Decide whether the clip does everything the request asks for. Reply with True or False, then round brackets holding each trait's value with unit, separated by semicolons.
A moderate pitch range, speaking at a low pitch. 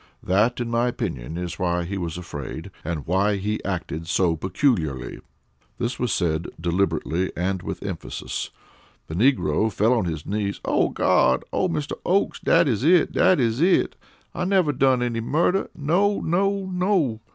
False (8.8 semitones; 105 Hz)